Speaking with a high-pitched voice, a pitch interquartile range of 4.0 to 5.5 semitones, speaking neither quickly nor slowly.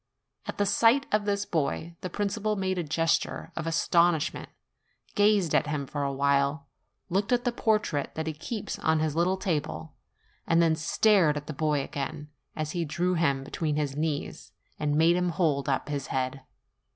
No: medium, 160 Hz; average, 4.3 semitones; average, 180 wpm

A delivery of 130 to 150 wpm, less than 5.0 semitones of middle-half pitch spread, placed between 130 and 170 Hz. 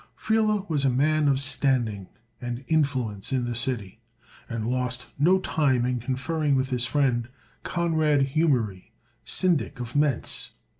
Yes: average, 140 wpm; average, 3.9 semitones; low, 135 Hz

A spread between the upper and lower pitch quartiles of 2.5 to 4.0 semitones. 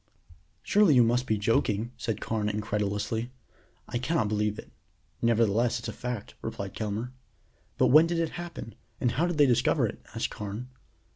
Yes: average, 3.2 semitones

